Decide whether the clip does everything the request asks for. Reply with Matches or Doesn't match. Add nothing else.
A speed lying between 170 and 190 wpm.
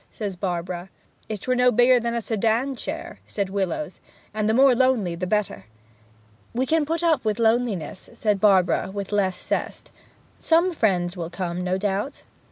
Matches